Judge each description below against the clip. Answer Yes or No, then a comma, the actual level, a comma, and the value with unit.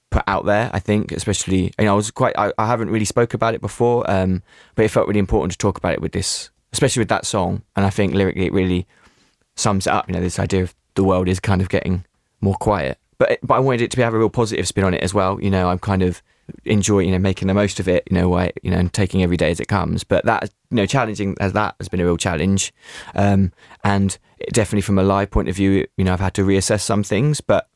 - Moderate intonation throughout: No, narrow, 2.3 semitones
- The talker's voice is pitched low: Yes, low, 100 Hz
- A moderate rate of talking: No, fast, 275 wpm